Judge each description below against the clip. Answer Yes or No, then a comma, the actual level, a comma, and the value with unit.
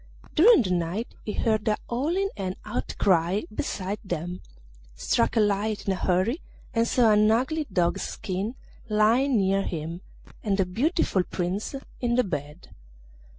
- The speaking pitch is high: Yes, high, 205 Hz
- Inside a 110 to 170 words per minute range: Yes, average, 150 wpm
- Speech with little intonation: No, average, 4.5 semitones